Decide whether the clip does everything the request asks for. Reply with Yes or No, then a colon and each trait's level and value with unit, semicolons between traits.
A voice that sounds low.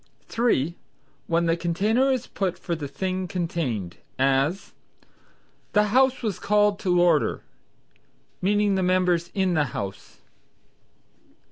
No: medium, 180 Hz